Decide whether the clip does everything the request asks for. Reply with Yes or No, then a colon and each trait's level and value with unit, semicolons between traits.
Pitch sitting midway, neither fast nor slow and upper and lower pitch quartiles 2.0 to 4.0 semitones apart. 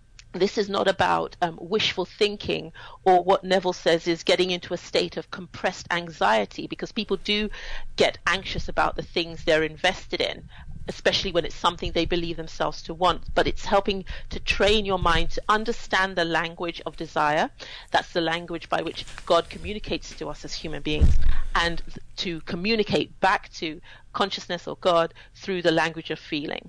Yes: medium, 175 Hz; average, 175 wpm; average, 2.9 semitones